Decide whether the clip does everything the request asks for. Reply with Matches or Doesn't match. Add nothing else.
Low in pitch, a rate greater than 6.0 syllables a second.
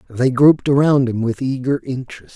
Doesn't match